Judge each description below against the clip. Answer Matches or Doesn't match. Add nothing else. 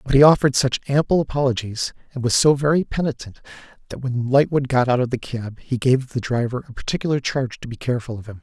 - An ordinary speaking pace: Doesn't match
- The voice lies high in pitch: Doesn't match